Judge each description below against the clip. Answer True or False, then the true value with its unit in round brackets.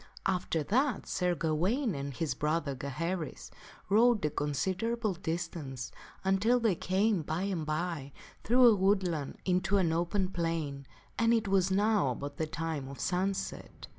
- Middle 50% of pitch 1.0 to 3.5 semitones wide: False (4.6 semitones)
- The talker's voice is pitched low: False (180 Hz)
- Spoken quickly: False (145 wpm)